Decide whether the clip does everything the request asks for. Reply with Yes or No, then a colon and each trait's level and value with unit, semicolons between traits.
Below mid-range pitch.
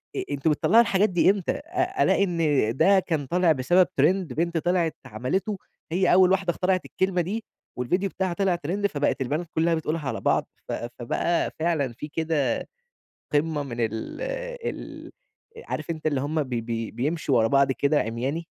No: medium, 165 Hz